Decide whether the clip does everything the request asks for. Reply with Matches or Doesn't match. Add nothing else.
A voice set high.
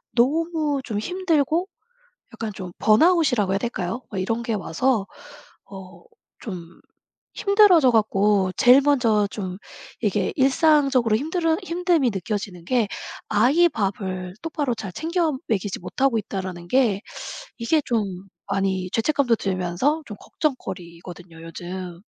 Matches